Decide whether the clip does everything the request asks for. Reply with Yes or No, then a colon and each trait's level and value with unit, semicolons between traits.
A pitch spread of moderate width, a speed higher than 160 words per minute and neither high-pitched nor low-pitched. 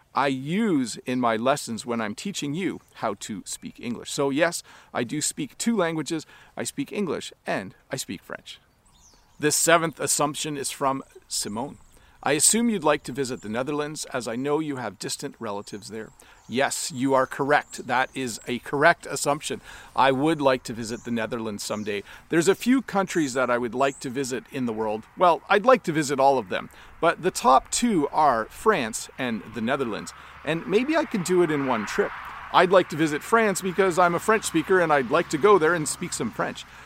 No: wide, 6.2 semitones; fast, 205 wpm; medium, 150 Hz